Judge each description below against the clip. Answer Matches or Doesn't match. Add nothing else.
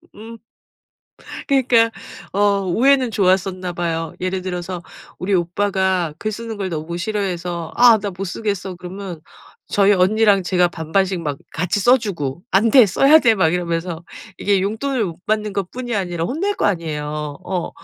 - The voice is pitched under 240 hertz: Matches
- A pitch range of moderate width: Matches